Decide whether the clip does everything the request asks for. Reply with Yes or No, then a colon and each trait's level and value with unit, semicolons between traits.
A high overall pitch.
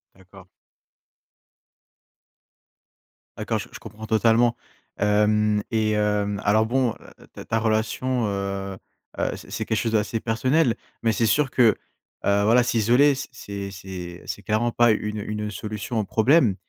No: low, 110 Hz